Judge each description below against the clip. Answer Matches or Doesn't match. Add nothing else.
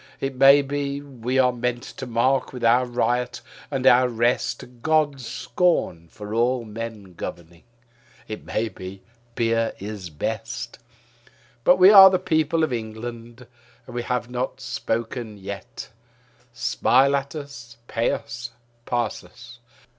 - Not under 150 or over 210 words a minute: Doesn't match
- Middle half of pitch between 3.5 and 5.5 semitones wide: Doesn't match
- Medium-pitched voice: Doesn't match